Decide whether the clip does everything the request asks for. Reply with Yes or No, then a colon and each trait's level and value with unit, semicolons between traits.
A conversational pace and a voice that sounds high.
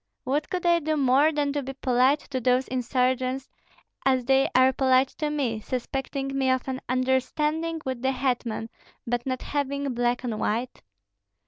Yes: average, 165 wpm; very high, 260 Hz